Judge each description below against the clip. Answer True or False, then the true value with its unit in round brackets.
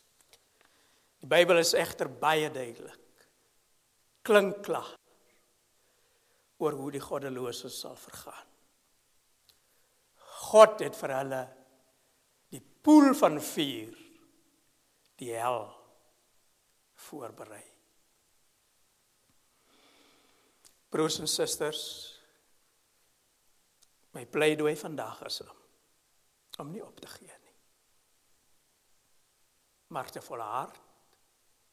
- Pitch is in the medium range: True (155 Hz)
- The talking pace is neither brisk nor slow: False (75 wpm)